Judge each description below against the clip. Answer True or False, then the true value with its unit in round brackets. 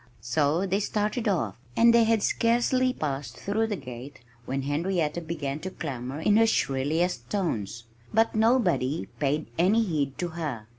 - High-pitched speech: False (165 Hz)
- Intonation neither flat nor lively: False (7.4 semitones)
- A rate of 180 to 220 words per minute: False (155 wpm)